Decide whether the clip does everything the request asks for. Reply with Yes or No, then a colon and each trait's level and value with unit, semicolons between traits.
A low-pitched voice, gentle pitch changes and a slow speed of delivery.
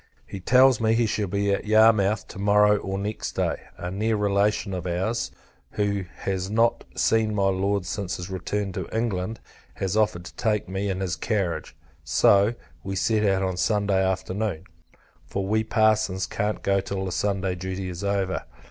No: low, 100 Hz; narrow, 2.2 semitones; average, 175 wpm